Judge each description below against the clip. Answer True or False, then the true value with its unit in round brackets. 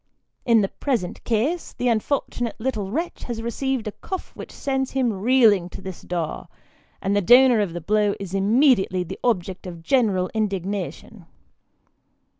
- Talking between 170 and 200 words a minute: False (155 wpm)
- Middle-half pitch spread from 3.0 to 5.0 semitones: True (4.6 semitones)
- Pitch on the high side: True (215 Hz)